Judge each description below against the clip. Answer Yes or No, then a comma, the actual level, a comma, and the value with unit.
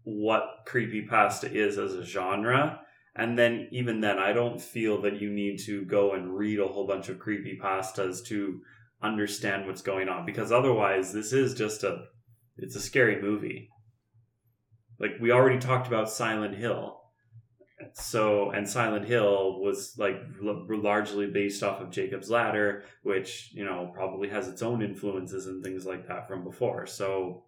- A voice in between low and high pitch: No, low, 105 Hz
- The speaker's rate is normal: Yes, average, 170 wpm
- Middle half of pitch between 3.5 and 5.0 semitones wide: No, average, 3.0 semitones